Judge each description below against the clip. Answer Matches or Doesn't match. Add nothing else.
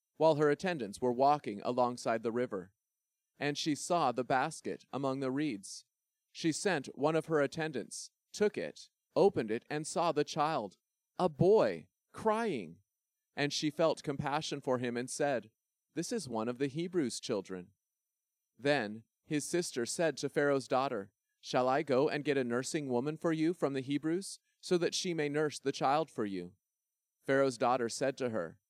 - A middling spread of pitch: Matches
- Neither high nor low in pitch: Matches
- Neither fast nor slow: Matches